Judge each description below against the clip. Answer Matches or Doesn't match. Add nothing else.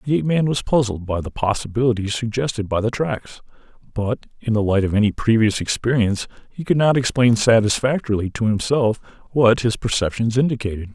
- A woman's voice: Doesn't match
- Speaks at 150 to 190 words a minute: Matches